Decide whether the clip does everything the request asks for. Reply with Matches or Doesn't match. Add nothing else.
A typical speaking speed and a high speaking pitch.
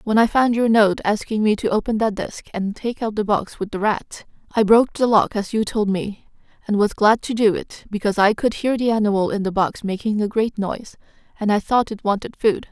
Doesn't match